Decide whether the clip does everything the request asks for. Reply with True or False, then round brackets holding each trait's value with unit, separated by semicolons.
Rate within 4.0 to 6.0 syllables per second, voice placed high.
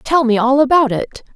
True (4.9 syllables/s; 265 Hz)